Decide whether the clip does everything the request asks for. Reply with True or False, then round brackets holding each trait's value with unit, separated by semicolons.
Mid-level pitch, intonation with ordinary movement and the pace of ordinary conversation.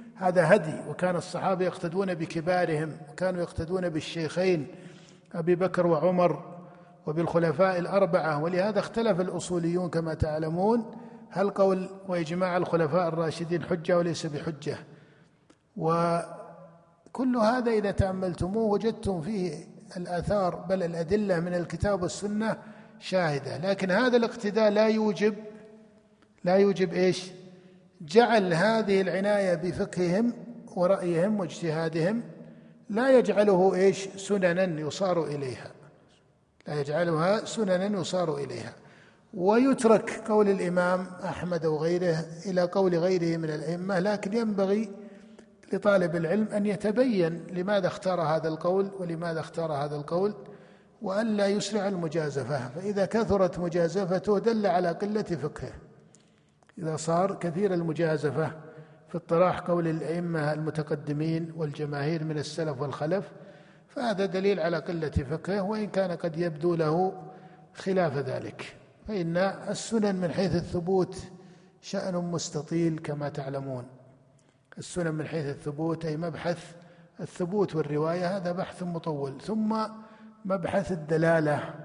True (180 Hz; 3.2 semitones; 110 wpm)